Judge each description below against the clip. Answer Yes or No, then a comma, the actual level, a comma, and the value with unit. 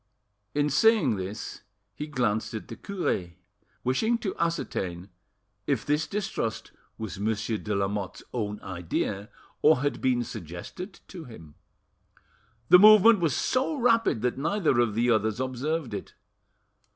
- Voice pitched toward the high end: No, low, 125 Hz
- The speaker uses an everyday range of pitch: No, wide, 8.1 semitones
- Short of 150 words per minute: Yes, slow, 135 wpm